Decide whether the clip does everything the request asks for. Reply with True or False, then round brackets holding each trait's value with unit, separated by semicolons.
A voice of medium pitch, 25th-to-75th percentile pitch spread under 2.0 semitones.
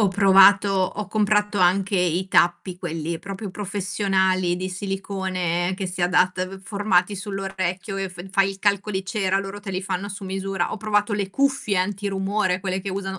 False (195 Hz; 1.5 semitones)